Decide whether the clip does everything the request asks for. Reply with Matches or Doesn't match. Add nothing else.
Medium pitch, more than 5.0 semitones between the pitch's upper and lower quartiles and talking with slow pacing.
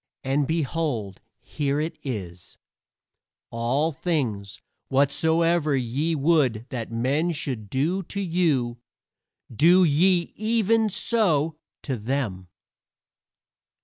Matches